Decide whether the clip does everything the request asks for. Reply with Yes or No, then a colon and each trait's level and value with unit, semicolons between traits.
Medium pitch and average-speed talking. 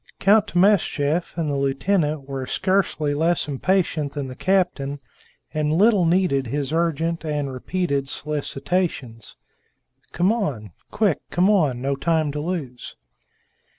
No: medium, 155 Hz; slow, 125 wpm